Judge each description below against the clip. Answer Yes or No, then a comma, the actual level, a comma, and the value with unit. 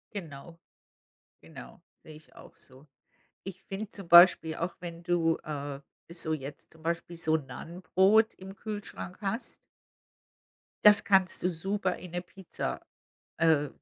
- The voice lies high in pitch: No, medium, 170 Hz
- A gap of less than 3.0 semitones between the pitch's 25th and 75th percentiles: No, average, 3.3 semitones